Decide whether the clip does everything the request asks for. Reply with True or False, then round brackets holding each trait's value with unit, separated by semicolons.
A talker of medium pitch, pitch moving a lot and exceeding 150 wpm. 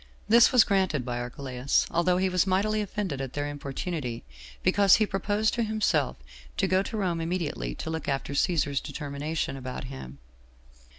True (160 Hz; 6.0 semitones; 165 wpm)